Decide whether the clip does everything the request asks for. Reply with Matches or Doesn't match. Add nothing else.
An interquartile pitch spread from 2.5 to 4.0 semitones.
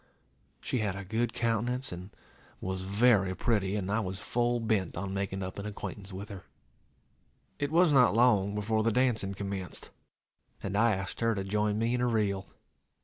Matches